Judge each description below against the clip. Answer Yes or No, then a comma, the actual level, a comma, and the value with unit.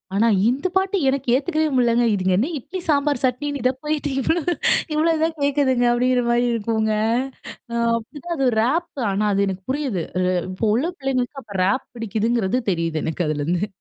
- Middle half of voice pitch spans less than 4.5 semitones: No, average, 5.1 semitones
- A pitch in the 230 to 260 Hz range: Yes, very high, 250 Hz